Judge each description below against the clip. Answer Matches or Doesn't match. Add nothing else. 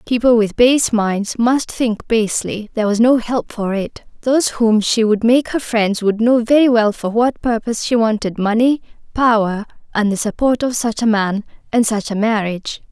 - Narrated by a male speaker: Doesn't match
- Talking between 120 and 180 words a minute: Doesn't match